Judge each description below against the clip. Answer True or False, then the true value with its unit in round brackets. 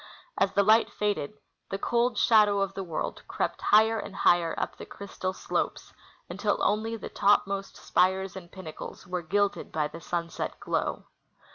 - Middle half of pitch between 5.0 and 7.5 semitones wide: False (2.8 semitones)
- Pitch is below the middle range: False (195 Hz)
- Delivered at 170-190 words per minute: False (160 wpm)